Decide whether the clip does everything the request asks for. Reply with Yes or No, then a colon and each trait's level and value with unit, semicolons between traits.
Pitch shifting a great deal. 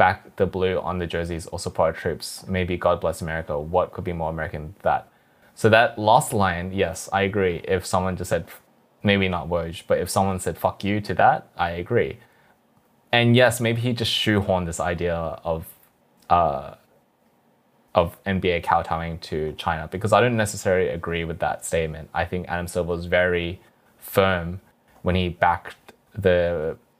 No: narrow, 2.5 semitones